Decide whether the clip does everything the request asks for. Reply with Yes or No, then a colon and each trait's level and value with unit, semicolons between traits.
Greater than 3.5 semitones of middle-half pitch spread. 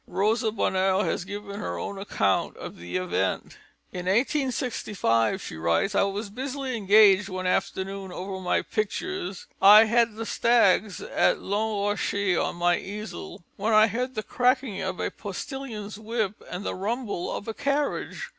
No: average, 3.2 semitones